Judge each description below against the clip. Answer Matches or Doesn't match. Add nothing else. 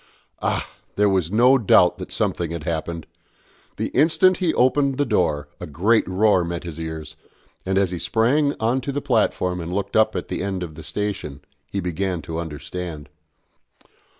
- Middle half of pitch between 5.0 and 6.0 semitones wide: Matches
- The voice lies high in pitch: Doesn't match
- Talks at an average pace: Matches